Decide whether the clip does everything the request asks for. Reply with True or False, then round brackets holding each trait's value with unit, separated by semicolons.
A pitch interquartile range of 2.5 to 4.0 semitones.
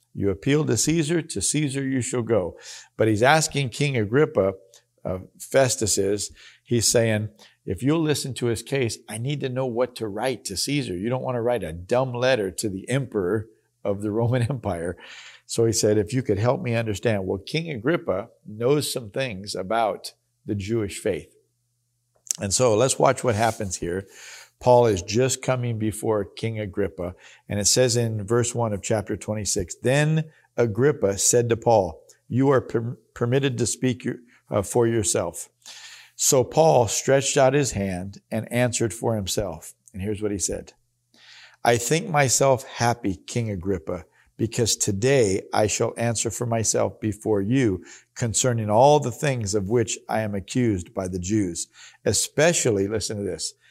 True (3.6 semitones)